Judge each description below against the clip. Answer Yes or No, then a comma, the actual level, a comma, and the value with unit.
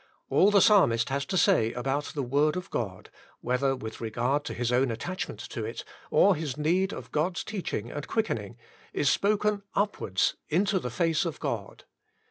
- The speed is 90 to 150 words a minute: No, average, 175 wpm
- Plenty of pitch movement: Yes, wide, 7.5 semitones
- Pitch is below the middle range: No, medium, 145 Hz